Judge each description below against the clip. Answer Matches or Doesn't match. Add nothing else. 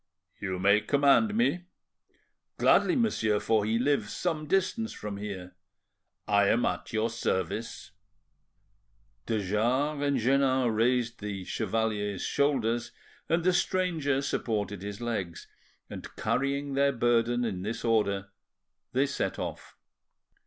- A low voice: Matches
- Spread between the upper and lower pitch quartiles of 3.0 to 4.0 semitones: Doesn't match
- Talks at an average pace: Doesn't match